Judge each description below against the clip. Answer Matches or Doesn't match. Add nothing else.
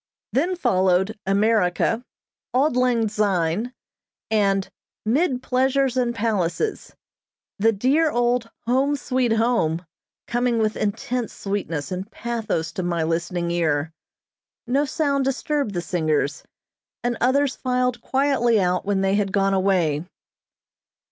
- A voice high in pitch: Matches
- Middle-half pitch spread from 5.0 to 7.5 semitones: Matches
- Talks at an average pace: Doesn't match